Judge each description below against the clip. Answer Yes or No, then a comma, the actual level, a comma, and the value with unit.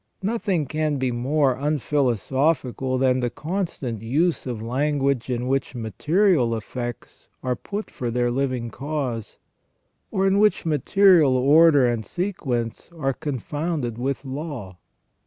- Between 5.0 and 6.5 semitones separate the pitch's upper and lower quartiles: No, average, 4.2 semitones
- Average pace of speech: No, slow, 125 wpm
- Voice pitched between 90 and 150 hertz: Yes, low, 135 Hz